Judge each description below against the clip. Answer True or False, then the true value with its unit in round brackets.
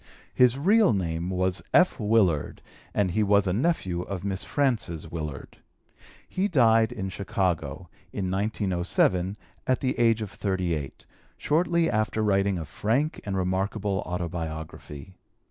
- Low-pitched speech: True (100 Hz)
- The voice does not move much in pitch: False (4.1 semitones)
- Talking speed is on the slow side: True (130 wpm)